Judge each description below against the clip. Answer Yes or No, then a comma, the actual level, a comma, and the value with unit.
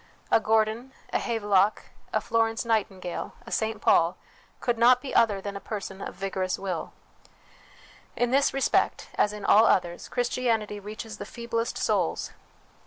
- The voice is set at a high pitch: Yes, high, 220 Hz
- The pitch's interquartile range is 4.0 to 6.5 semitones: No, average, 2.8 semitones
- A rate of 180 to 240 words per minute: No, average, 155 wpm